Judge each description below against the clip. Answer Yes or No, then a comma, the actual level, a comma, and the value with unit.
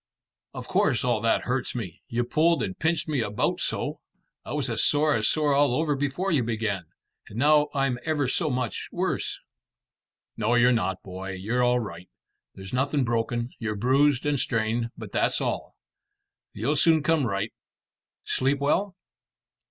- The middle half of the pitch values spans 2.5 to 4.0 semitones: No, average, 4.6 semitones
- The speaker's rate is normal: Yes, average, 165 wpm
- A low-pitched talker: Yes, low, 125 Hz